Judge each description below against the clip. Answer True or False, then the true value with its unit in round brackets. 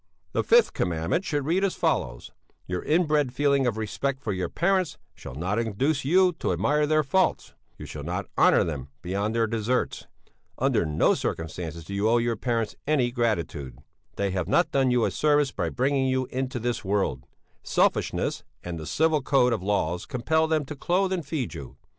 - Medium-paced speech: True (185 wpm)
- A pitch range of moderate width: False (7.2 semitones)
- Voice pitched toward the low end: True (125 Hz)